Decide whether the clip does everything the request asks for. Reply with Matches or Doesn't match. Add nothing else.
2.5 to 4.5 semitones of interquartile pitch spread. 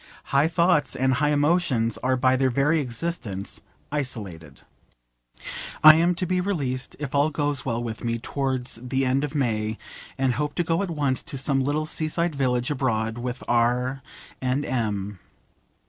Matches